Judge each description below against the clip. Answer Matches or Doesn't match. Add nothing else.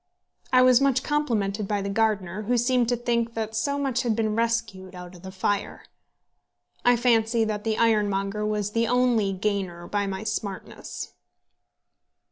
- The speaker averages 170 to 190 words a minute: Doesn't match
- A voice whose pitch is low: Doesn't match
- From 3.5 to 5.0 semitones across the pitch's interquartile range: Doesn't match